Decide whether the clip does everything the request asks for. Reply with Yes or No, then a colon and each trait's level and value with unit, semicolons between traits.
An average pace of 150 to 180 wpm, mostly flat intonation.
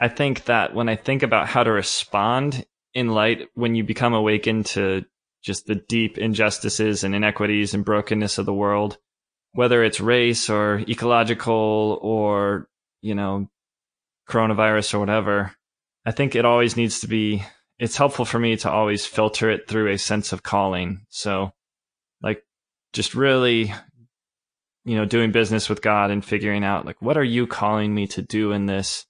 Yes: average, 170 wpm; narrow, 2.2 semitones